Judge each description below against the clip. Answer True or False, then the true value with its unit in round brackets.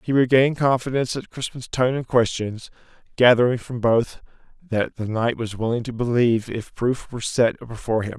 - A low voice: True (120 Hz)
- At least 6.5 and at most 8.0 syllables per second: False (5.5 syllables/s)